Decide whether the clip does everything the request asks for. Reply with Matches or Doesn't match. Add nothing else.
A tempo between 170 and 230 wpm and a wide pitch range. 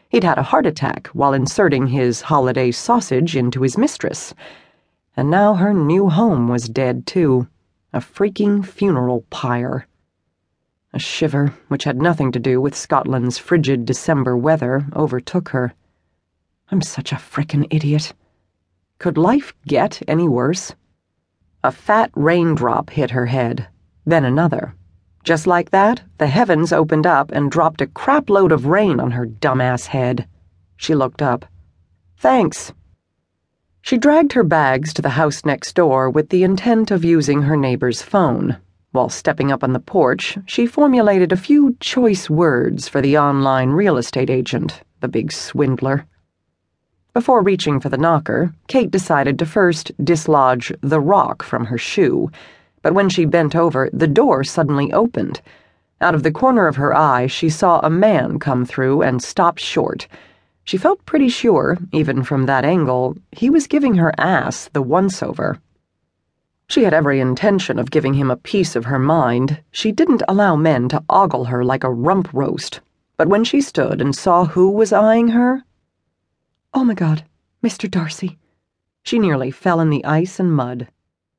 Doesn't match